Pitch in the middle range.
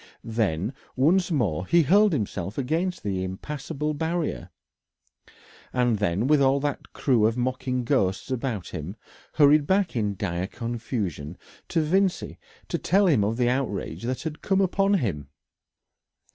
No: low, 125 Hz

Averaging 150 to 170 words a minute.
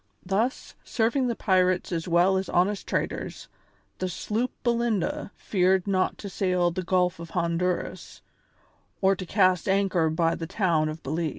Yes: average, 155 wpm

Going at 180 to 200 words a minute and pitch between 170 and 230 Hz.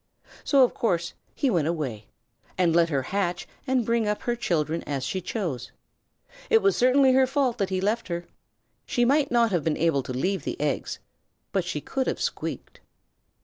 Yes: average, 190 wpm; high, 190 Hz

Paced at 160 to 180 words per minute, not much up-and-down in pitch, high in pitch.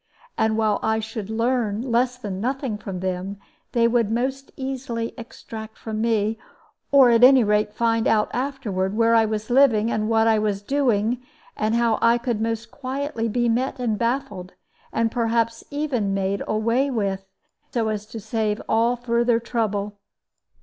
Yes: average, 165 wpm; narrow, 2.3 semitones; high, 230 Hz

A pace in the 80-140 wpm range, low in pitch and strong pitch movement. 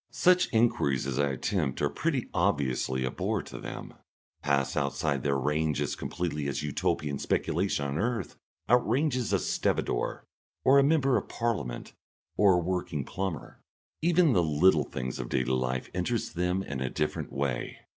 No: average, 160 wpm; very low, 75 Hz; wide, 8.2 semitones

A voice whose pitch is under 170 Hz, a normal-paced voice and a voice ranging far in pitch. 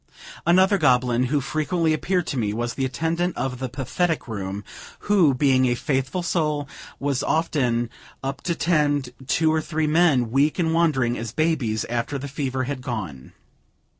No: medium, 140 Hz; average, 165 wpm; average, 4.6 semitones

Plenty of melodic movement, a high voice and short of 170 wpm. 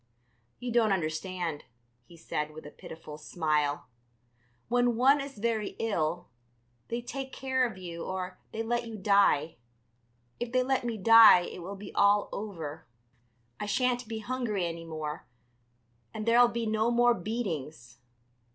Yes: wide, 6.2 semitones; high, 205 Hz; average, 150 wpm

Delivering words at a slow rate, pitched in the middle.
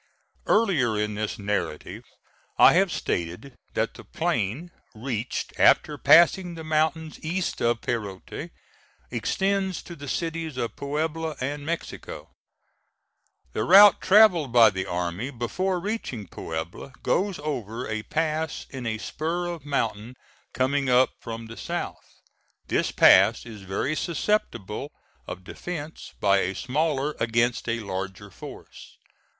No: slow, 130 wpm; low, 130 Hz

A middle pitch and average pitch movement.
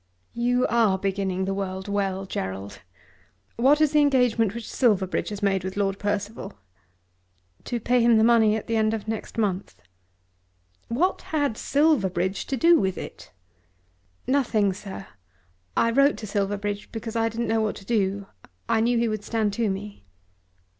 No: high, 215 Hz; average, 3.2 semitones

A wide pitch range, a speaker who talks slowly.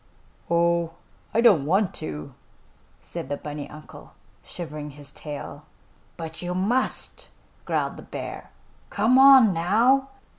Yes: wide, 6.6 semitones; slow, 120 wpm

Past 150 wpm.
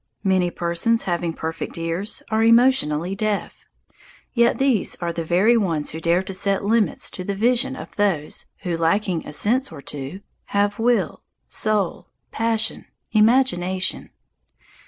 No: average, 140 wpm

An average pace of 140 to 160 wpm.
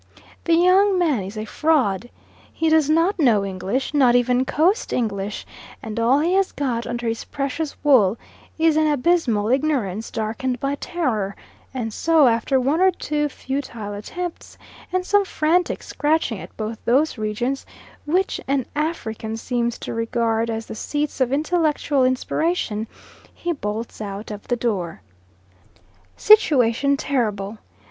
Yes: average, 145 wpm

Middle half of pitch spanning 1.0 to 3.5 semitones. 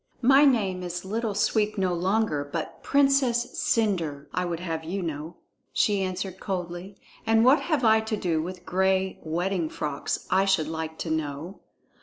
No: average, 4.5 semitones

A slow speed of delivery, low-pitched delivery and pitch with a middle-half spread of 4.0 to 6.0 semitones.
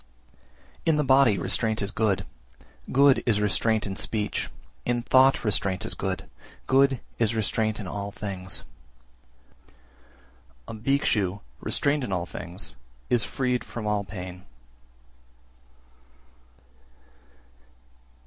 Yes: slow, 110 wpm; low, 110 Hz; average, 4.3 semitones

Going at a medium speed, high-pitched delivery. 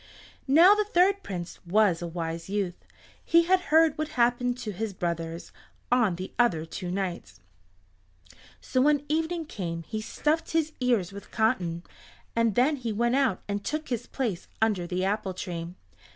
Yes: average, 165 wpm; high, 220 Hz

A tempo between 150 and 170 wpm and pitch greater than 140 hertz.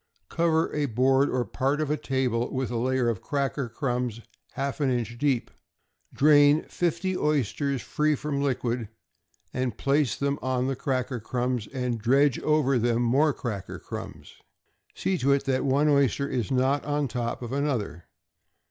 No: average, 155 wpm; low, 135 Hz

